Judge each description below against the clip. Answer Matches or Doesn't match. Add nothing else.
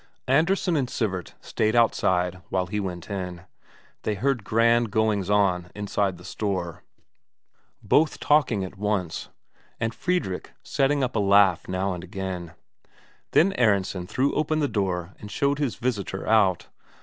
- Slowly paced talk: Doesn't match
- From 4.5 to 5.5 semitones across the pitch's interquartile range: Matches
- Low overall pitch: Matches